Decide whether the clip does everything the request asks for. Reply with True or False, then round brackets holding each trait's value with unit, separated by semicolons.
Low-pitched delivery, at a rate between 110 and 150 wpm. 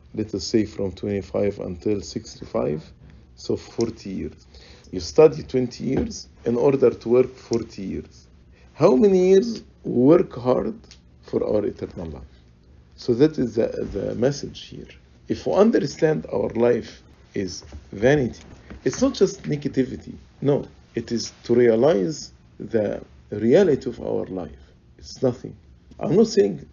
True (100 Hz; 140 wpm)